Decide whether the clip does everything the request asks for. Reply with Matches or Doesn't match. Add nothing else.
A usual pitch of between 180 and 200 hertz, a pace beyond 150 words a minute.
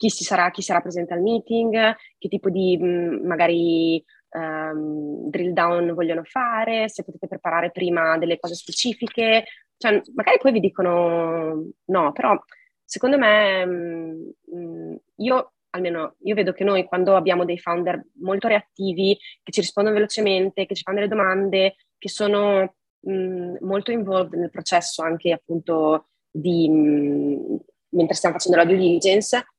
Doesn't match